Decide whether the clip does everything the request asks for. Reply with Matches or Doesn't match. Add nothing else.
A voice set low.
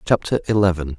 Matches